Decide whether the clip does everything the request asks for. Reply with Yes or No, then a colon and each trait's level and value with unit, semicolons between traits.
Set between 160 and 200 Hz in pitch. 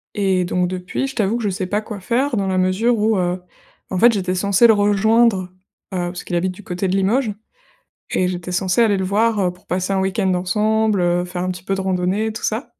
Yes: high, 190 Hz